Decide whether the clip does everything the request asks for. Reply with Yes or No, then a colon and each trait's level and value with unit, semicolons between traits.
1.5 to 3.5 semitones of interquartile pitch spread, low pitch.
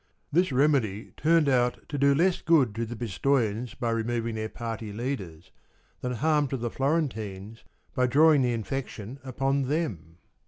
No: average, 4.1 semitones; low, 125 Hz